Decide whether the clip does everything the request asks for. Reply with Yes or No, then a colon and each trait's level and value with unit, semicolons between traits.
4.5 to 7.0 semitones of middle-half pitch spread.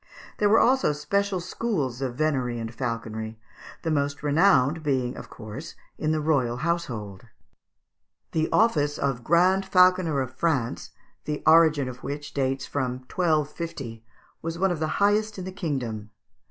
Yes: average, 5.1 semitones